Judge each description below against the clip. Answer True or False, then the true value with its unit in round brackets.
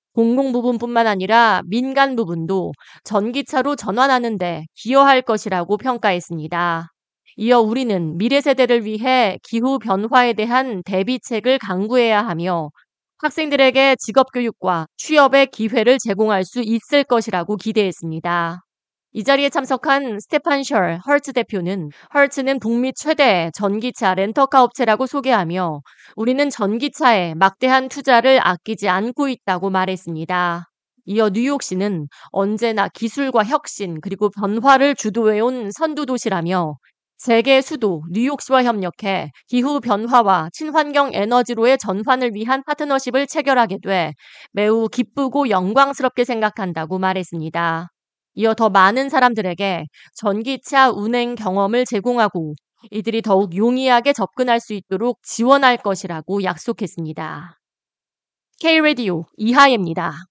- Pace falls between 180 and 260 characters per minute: False (310 characters per minute)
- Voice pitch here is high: True (225 Hz)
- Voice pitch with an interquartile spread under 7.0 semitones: True (5.4 semitones)